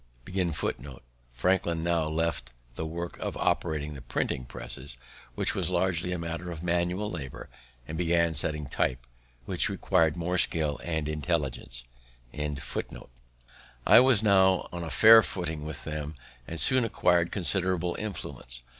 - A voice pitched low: Yes, very low, 85 Hz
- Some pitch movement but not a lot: Yes, average, 3.3 semitones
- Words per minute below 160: Yes, slow, 135 wpm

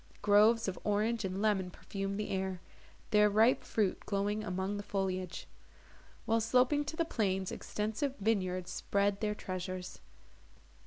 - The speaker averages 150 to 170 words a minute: No, average, 140 wpm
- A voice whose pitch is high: Yes, high, 205 Hz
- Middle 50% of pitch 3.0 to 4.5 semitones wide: No, narrow, 2.4 semitones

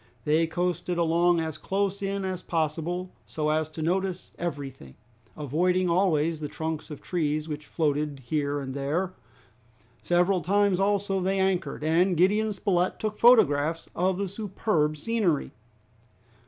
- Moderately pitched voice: Yes, medium, 175 Hz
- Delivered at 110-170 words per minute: Yes, average, 140 wpm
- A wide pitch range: No, average, 3.8 semitones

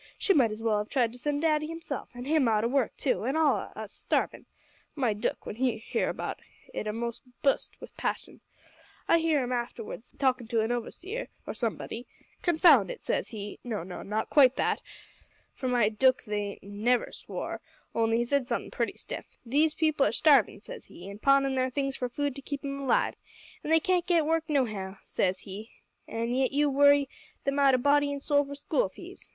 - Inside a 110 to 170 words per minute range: No, average, 200 wpm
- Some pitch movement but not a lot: Yes, average, 4.1 semitones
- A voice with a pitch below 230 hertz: No, very high, 260 Hz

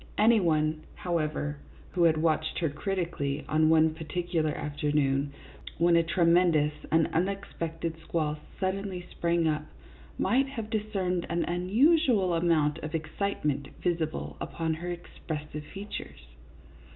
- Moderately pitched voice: Yes, medium, 165 Hz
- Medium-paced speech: No, slow, 130 wpm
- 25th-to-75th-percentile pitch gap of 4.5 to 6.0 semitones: No, average, 2.9 semitones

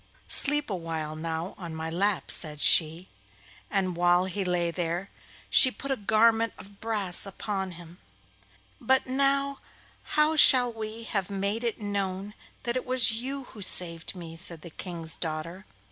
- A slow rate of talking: No, average, 160 wpm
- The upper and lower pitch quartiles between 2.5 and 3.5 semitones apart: No, average, 5.0 semitones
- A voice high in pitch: Yes, high, 195 Hz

